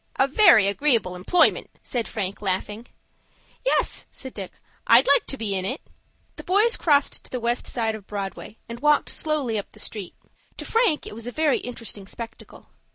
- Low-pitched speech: No, high, 235 Hz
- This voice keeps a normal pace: Yes, average, 180 wpm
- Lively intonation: Yes, wide, 5.8 semitones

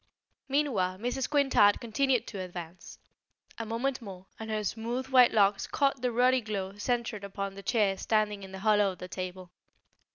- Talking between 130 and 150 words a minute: No, average, 170 wpm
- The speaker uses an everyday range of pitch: Yes, average, 4.2 semitones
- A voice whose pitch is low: No, high, 215 Hz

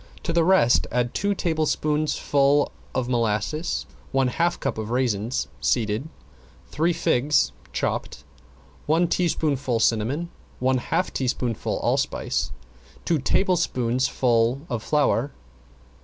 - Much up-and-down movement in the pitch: No, average, 4.6 semitones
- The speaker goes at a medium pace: No, slow, 105 wpm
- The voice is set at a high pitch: No, low, 135 Hz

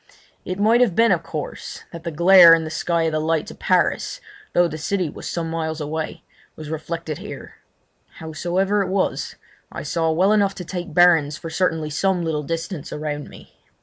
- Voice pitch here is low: No, medium, 165 Hz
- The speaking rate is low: No, average, 190 wpm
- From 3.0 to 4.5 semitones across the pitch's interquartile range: No, narrow, 2.6 semitones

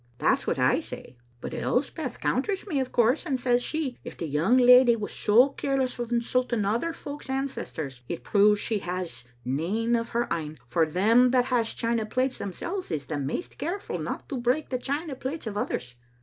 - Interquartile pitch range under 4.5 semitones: No, average, 4.8 semitones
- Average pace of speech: Yes, average, 190 wpm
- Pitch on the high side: Yes, high, 240 Hz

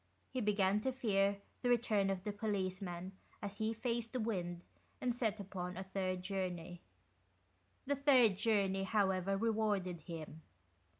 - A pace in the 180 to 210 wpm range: No, average, 140 wpm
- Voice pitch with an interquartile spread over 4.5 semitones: No, average, 3.1 semitones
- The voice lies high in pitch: Yes, high, 200 Hz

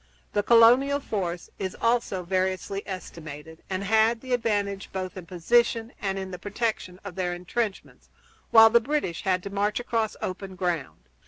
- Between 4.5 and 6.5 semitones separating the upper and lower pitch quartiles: No, average, 3.7 semitones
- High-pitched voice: Yes, high, 195 Hz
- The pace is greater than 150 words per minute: Yes, average, 160 wpm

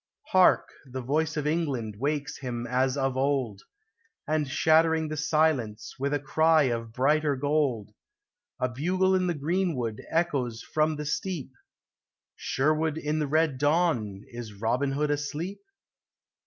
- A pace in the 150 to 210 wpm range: No, average, 140 wpm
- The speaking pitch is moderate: Yes, medium, 145 Hz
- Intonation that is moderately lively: Yes, average, 3.7 semitones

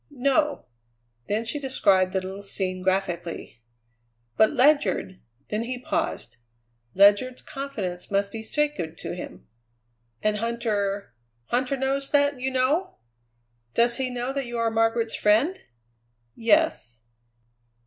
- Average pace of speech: No, slow, 125 wpm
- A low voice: No, high, 230 Hz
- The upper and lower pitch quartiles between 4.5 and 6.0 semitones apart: Yes, average, 5.3 semitones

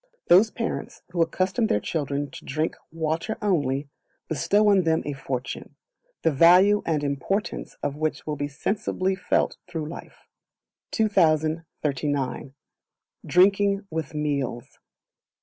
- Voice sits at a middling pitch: Yes, medium, 160 Hz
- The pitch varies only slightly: No, average, 4.7 semitones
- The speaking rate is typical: No, slow, 120 wpm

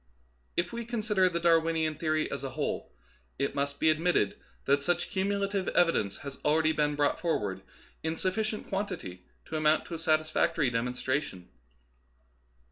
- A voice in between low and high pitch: Yes, medium, 160 Hz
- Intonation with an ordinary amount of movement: Yes, average, 4.1 semitones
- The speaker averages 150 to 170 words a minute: Yes, average, 160 wpm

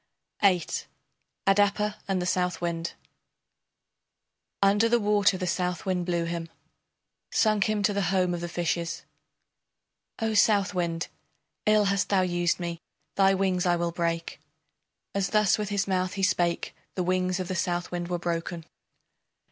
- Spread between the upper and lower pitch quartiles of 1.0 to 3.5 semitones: Yes, narrow, 2.5 semitones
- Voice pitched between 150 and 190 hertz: Yes, medium, 185 Hz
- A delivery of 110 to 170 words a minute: Yes, average, 145 wpm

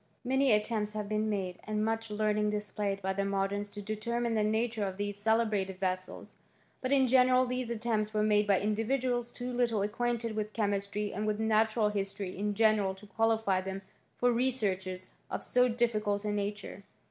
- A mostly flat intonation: Yes, narrow, 2.3 semitones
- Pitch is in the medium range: No, high, 215 Hz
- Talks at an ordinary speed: Yes, average, 175 wpm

